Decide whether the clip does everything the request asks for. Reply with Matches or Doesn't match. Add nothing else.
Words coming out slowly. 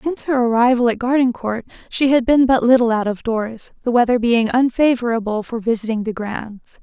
Doesn't match